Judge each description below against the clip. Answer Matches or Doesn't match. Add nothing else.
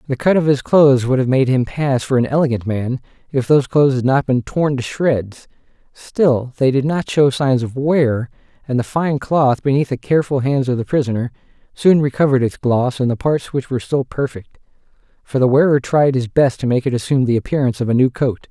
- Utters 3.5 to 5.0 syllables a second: Doesn't match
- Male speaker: Matches